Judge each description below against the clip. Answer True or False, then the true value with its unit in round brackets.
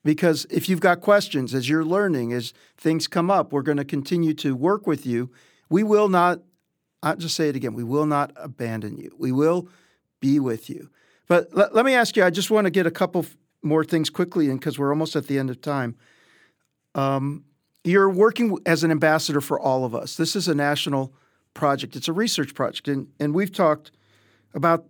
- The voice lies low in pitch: False (155 Hz)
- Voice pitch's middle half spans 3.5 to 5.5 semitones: True (4.0 semitones)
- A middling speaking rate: False (210 wpm)